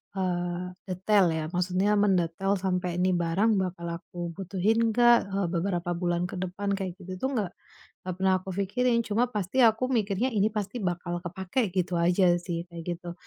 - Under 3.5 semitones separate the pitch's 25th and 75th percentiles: Yes, average, 2.7 semitones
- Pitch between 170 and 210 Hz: Yes, medium, 185 Hz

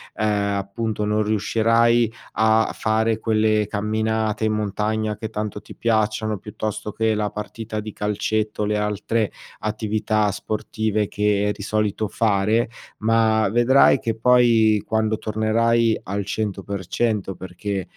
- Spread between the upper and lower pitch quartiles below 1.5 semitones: Yes, narrow, 1.0 semitones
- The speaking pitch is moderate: No, low, 110 Hz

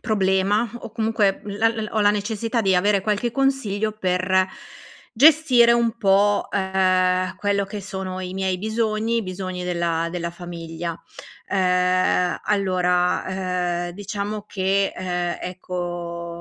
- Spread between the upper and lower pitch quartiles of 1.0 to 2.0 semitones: No, average, 2.7 semitones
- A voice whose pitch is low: No, high, 190 Hz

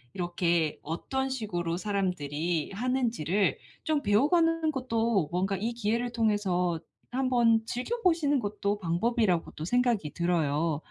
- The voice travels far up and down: Yes, wide, 6.0 semitones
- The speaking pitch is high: Yes, high, 210 Hz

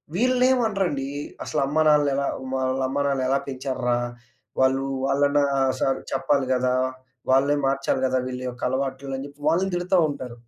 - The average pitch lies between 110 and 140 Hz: Yes, low, 135 Hz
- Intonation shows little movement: Yes, narrow, 2.0 semitones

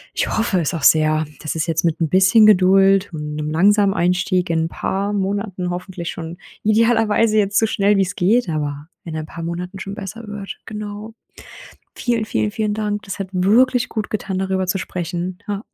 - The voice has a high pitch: Yes, high, 195 Hz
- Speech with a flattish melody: No, average, 3.4 semitones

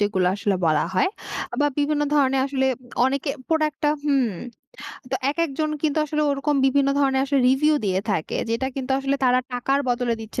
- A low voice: No, very high, 270 Hz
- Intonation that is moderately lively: Yes, average, 3.0 semitones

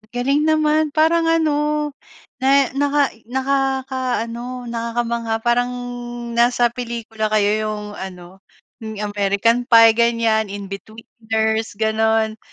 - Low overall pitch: No, high, 235 Hz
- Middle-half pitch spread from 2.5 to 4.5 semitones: Yes, average, 3.5 semitones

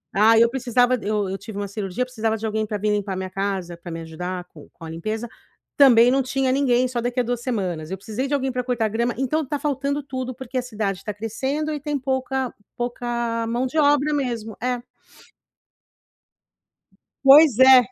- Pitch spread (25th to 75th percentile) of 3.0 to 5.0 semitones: Yes, average, 3.8 semitones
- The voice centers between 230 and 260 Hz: Yes, high, 240 Hz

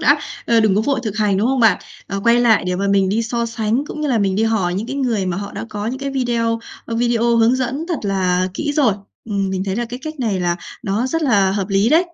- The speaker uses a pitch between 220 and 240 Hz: Yes, high, 225 Hz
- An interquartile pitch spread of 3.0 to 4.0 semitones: Yes, average, 3.7 semitones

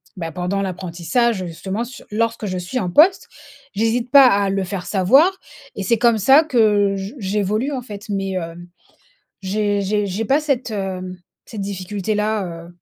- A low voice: No, high, 205 Hz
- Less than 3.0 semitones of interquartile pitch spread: No, average, 3.6 semitones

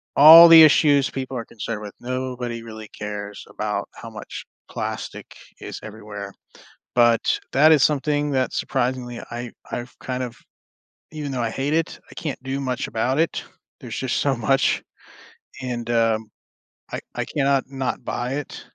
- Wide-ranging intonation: No, average, 3.1 semitones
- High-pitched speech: No, low, 130 Hz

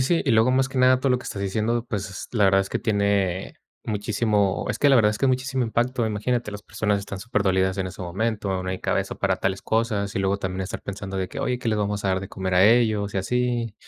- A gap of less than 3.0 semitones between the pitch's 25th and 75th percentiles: No, average, 3.5 semitones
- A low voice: Yes, low, 105 Hz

